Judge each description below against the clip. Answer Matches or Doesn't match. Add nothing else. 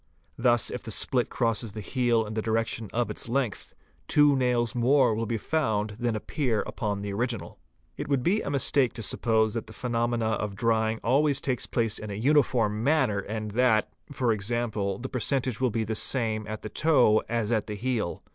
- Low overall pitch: Matches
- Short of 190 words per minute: Doesn't match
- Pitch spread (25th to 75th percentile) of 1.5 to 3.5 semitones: Matches